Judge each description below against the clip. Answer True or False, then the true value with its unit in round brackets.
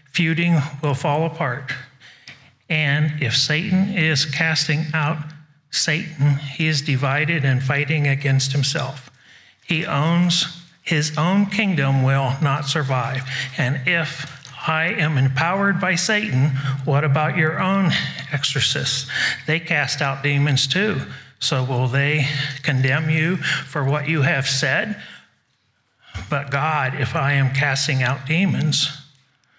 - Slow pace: True (125 wpm)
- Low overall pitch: False (145 Hz)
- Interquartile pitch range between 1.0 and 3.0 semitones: True (2.7 semitones)